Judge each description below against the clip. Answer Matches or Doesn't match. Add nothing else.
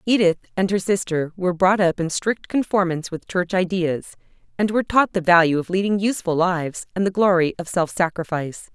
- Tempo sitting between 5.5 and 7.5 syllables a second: Matches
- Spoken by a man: Doesn't match